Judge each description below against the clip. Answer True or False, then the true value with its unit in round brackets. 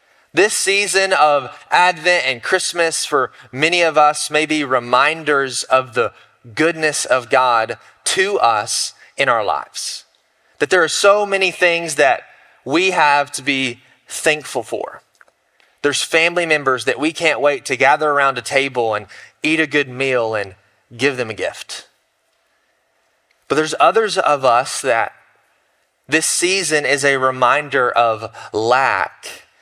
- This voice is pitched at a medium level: True (150 Hz)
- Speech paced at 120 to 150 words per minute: True (145 wpm)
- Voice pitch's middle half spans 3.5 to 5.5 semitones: True (5.1 semitones)